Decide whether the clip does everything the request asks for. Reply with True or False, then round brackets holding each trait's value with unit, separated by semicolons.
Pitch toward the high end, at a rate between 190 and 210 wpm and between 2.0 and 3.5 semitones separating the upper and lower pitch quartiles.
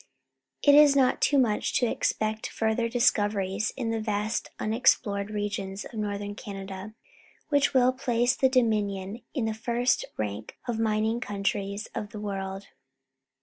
False (215 Hz; 150 wpm; 3.0 semitones)